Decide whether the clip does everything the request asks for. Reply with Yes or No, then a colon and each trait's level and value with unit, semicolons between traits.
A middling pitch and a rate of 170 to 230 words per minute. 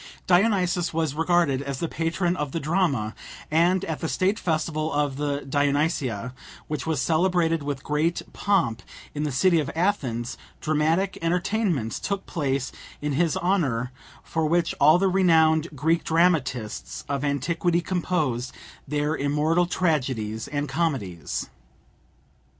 No: medium, 155 Hz; slow, 135 wpm